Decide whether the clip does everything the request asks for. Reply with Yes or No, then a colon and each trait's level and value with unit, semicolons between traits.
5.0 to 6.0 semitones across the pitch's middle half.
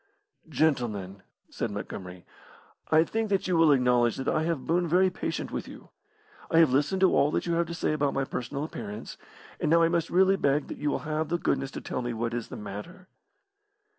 Yes: wide, 5.6 semitones